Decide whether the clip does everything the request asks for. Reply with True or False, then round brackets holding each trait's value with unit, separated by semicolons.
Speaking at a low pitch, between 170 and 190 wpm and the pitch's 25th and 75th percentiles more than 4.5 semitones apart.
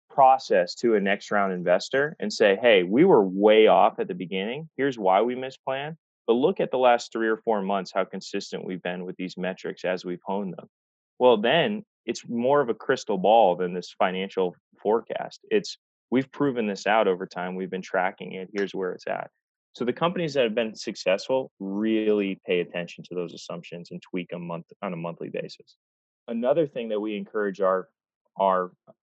False (100 Hz; 200 wpm; 5.3 semitones)